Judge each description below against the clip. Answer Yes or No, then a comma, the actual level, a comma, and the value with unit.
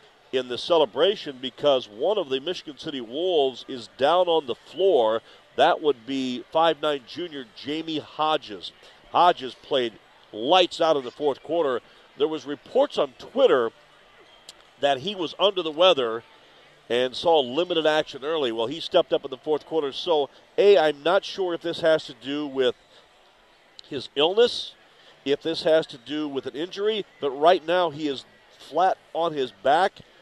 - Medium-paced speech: Yes, average, 165 wpm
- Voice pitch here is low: No, medium, 155 Hz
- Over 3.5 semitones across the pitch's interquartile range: Yes, average, 4.4 semitones